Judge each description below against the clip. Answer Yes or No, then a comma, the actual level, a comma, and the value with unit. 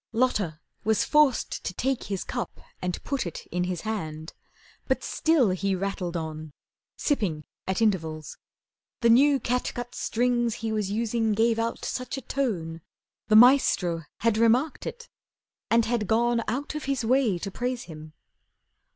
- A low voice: No, high, 225 Hz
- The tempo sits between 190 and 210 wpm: No, average, 150 wpm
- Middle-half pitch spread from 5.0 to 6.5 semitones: Yes, average, 5.3 semitones